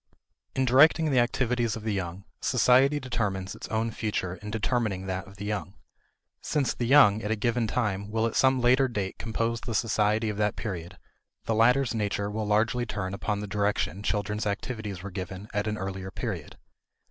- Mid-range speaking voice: No, low, 105 Hz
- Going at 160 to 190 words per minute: Yes, average, 185 wpm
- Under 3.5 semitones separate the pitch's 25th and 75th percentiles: Yes, average, 3.0 semitones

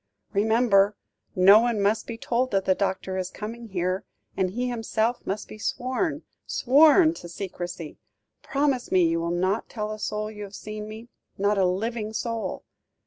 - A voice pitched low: No, high, 215 Hz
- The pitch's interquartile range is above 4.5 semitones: No, average, 3.7 semitones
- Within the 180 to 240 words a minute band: No, average, 170 wpm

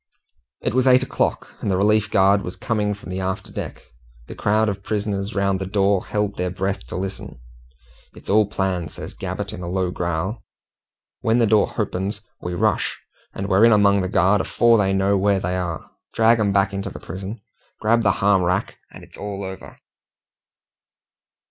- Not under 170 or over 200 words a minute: Yes, average, 185 wpm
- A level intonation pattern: Yes, narrow, 1.8 semitones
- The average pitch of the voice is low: Yes, low, 100 Hz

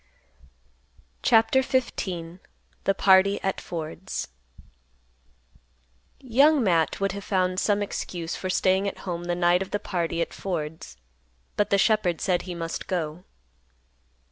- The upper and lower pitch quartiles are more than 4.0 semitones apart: No, average, 2.7 semitones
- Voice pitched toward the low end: No, medium, 185 Hz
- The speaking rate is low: Yes, slow, 130 wpm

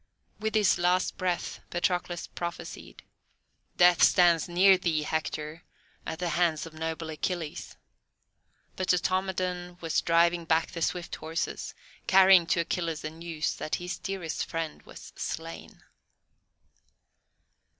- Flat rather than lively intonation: Yes, narrow, 1.9 semitones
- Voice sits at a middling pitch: Yes, medium, 170 Hz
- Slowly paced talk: Yes, slow, 120 wpm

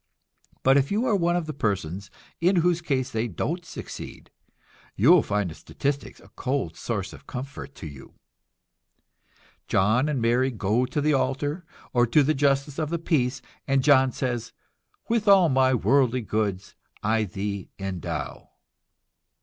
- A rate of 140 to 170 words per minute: Yes, average, 160 wpm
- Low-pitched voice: Yes, low, 130 Hz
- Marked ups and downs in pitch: Yes, wide, 5.7 semitones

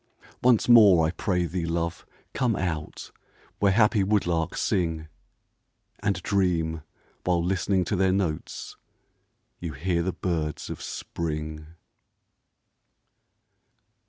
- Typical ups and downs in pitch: Yes, average, 3.0 semitones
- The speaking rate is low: Yes, slow, 105 wpm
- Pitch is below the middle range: Yes, very low, 90 Hz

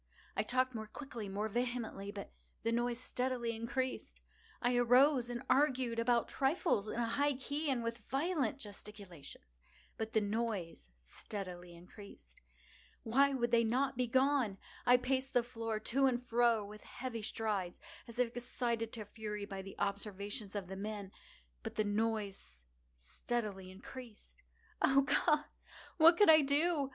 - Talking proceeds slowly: No, average, 145 wpm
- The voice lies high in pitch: Yes, high, 230 Hz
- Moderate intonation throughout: Yes, average, 3.9 semitones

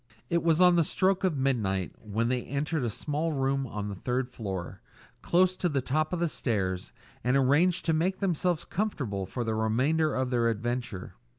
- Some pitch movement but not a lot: No, wide, 6.6 semitones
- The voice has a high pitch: No, low, 135 Hz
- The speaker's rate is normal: Yes, average, 190 wpm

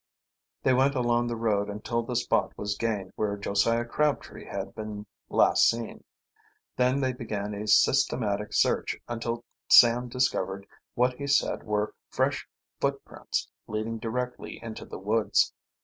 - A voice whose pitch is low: Yes, low, 115 Hz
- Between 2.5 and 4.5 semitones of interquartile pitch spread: Yes, average, 2.9 semitones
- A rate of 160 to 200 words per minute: No, average, 140 wpm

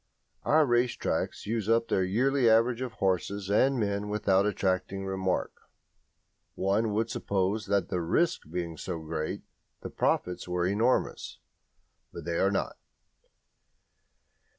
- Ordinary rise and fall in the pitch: Yes, average, 3.6 semitones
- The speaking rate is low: Yes, slow, 130 wpm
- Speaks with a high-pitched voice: No, low, 100 Hz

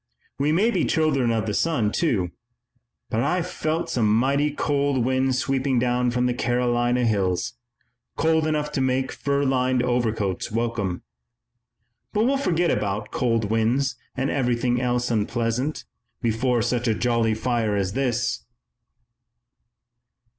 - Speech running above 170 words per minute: No, slow, 135 wpm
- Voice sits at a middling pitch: No, low, 125 Hz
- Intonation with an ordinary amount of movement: Yes, average, 3.4 semitones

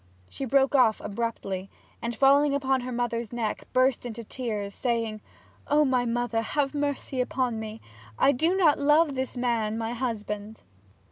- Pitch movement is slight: No, average, 3.3 semitones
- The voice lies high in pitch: Yes, high, 245 Hz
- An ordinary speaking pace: Yes, average, 155 wpm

